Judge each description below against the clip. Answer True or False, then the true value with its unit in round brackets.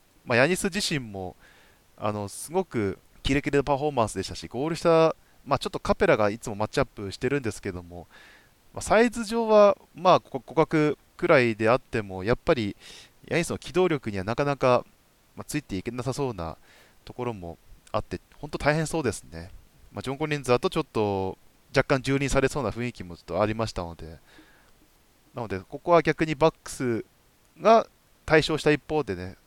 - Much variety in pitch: True (7.4 semitones)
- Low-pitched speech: True (125 Hz)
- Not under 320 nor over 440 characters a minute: True (365 characters per minute)